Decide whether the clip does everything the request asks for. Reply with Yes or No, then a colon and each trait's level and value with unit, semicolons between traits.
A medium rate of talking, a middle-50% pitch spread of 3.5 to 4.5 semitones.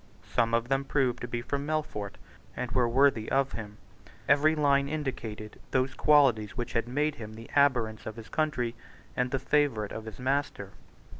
Yes: average, 175 wpm; average, 3.9 semitones